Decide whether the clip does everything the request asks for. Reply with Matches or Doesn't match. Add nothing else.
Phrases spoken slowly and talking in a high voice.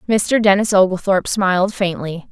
Matches